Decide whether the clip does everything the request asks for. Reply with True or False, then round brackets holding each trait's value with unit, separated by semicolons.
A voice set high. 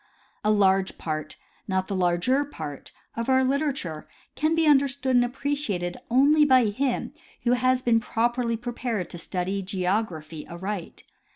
True (230 Hz)